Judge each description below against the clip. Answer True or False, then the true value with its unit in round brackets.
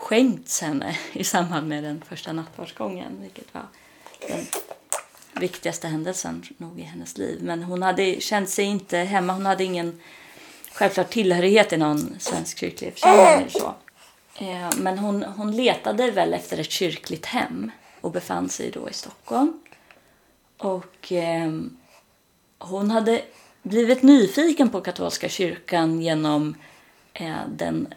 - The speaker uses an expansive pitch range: False (4.3 semitones)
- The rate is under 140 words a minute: True (125 wpm)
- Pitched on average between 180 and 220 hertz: True (185 Hz)